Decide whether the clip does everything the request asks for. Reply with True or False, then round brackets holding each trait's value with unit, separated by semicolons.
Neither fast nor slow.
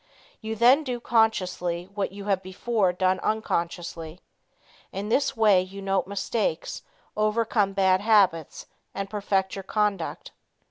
False (130 wpm)